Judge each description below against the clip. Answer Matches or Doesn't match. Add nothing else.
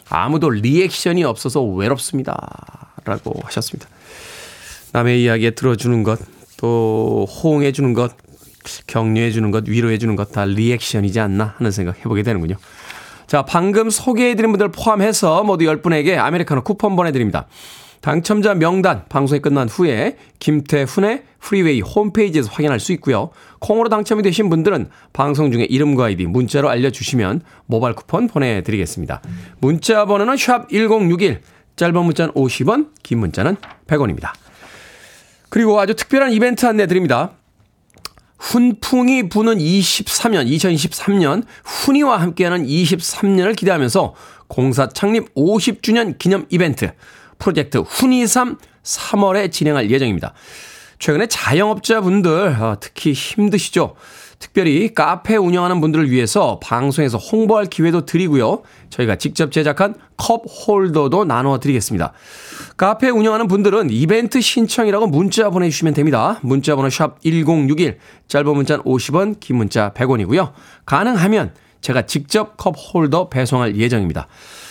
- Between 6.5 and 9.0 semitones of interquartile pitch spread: Matches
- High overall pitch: Doesn't match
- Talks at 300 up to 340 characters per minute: Matches